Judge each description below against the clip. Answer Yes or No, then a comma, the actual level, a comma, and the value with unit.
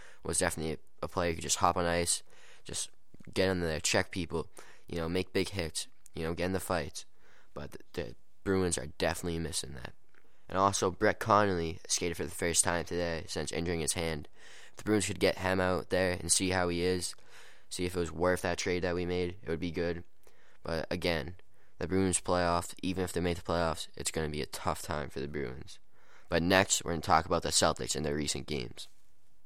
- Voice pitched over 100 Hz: No, very low, 85 Hz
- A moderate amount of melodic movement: No, narrow, 1.9 semitones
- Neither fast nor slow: No, fast, 220 wpm